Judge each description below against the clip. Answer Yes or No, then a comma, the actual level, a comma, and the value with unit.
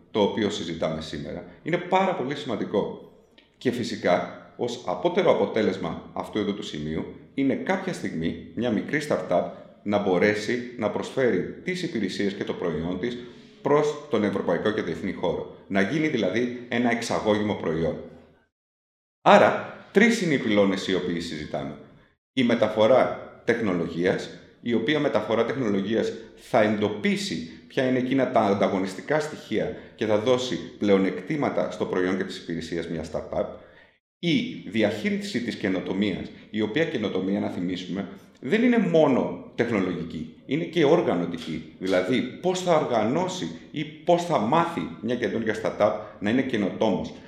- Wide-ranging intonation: Yes, wide, 7.8 semitones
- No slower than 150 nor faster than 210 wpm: No, average, 135 wpm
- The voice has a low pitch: Yes, low, 110 Hz